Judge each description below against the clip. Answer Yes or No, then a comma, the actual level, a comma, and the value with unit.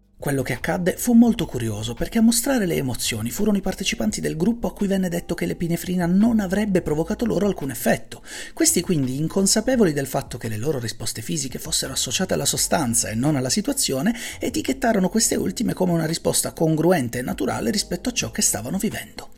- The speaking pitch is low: No, medium, 180 Hz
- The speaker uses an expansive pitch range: Yes, wide, 7.7 semitones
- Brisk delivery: Yes, fast, 190 wpm